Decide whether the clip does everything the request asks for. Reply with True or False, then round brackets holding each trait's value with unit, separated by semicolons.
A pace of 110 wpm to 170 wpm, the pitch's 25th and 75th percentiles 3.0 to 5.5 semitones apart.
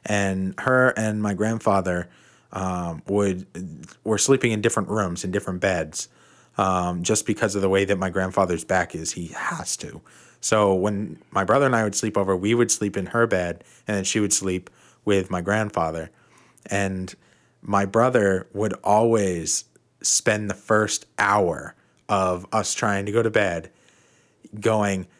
False (165 wpm; 2.5 semitones)